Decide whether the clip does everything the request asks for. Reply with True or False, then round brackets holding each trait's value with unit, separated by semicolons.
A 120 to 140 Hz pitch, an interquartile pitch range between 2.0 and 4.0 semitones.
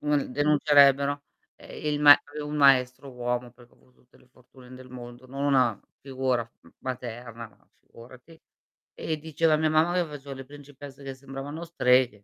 True (135 Hz; 2.6 semitones)